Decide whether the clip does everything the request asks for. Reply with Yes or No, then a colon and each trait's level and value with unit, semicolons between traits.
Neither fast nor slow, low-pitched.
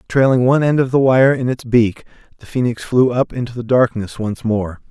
No: fast, 220 wpm; low, 120 Hz